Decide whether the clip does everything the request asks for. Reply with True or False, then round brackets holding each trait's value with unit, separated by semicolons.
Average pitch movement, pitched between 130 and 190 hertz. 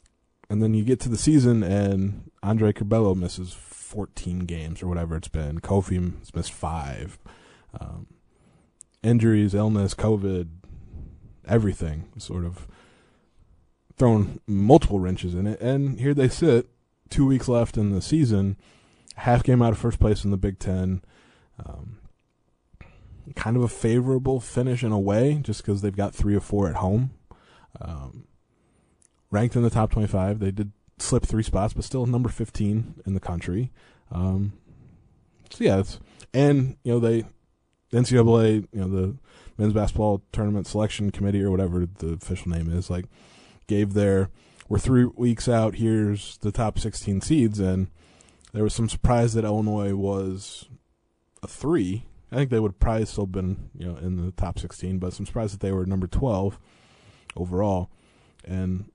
False (3.6 semitones; 100 Hz)